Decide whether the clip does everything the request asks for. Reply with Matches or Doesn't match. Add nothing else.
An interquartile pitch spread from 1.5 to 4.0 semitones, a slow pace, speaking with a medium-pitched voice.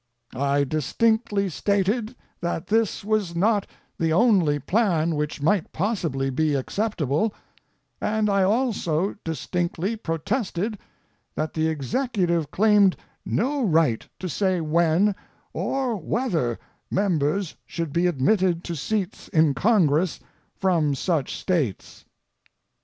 Doesn't match